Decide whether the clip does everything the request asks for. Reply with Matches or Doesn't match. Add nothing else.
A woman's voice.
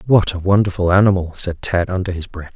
Doesn't match